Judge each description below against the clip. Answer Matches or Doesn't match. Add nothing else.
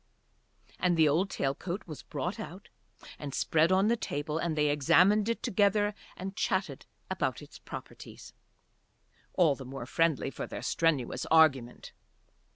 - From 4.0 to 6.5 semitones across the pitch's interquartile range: Matches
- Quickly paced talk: Doesn't match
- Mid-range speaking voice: Matches